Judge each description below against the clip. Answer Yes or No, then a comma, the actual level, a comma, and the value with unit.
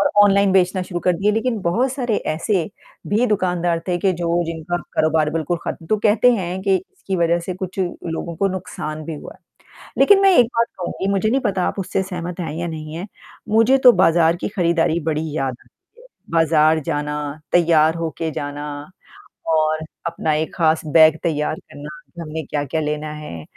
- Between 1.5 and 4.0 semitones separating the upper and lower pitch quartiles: Yes, average, 3.5 semitones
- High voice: No, medium, 170 Hz